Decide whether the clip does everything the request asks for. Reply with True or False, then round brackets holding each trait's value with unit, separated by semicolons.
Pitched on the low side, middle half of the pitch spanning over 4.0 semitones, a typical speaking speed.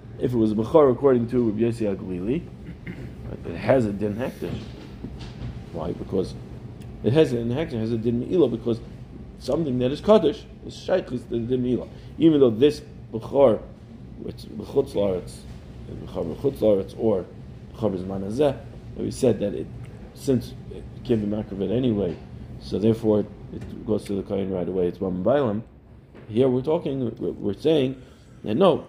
False (115 Hz; 3.4 semitones; 160 wpm)